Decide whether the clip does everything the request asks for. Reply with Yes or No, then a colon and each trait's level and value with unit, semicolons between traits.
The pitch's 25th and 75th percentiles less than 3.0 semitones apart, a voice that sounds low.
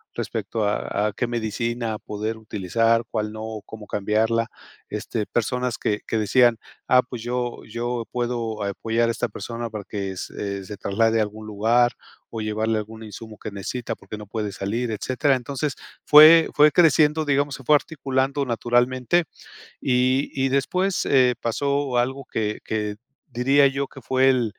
No: average, 3.3 semitones; low, 115 Hz